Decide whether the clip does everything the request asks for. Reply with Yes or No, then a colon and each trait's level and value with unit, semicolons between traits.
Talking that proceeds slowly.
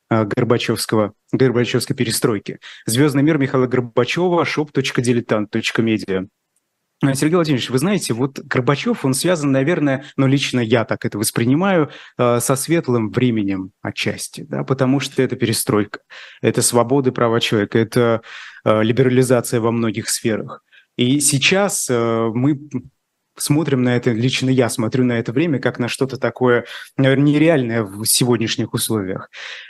No: average, 125 wpm